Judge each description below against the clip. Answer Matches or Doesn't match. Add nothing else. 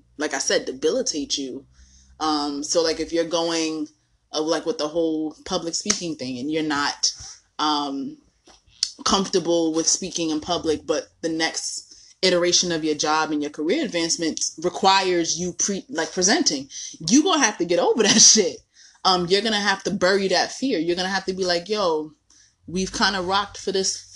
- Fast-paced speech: Doesn't match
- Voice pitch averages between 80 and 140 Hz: Doesn't match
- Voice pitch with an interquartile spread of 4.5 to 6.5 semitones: Doesn't match